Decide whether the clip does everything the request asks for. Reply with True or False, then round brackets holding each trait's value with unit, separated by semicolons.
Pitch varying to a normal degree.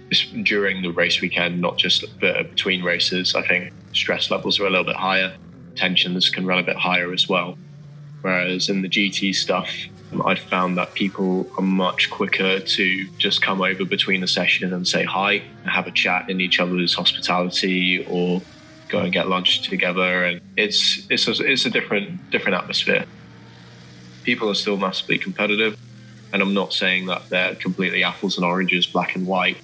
False (1.3 semitones)